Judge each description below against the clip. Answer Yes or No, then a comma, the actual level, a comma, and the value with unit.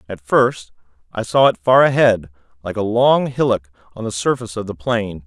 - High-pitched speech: No, low, 110 Hz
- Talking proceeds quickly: No, average, 195 wpm